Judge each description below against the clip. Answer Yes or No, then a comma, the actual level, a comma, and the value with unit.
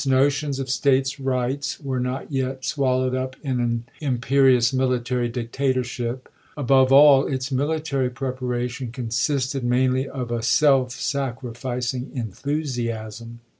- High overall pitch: No, low, 130 Hz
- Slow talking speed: Yes, slow, 115 wpm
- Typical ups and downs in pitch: No, narrow, 1.9 semitones